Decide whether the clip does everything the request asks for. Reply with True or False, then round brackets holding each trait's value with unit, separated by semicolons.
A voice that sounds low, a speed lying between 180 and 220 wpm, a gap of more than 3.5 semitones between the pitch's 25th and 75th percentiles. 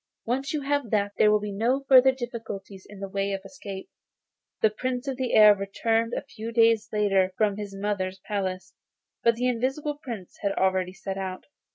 False (210 Hz; 190 wpm; 4.0 semitones)